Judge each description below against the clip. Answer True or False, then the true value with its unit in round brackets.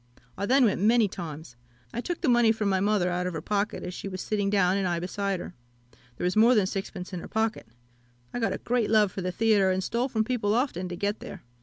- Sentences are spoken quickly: True (255 wpm)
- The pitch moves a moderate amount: True (3.5 semitones)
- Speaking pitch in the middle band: False (200 Hz)